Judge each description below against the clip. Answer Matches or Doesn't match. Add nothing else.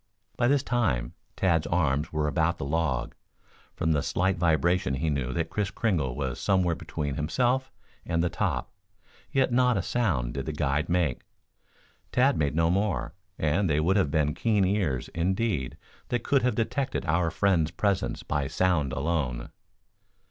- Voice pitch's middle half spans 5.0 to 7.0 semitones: Matches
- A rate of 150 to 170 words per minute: Matches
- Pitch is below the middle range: Matches